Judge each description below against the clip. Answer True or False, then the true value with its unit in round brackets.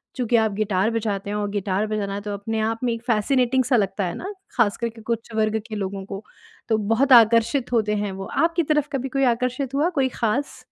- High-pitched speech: True (225 Hz)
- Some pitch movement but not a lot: True (3.4 semitones)